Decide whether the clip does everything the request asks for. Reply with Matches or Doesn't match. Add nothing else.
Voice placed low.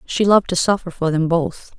Doesn't match